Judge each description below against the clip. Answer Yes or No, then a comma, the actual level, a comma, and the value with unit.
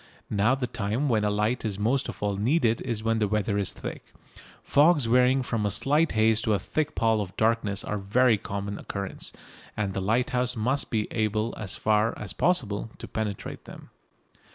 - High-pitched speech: No, low, 110 Hz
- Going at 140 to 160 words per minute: No, average, 200 wpm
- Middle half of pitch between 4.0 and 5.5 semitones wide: No, average, 3.3 semitones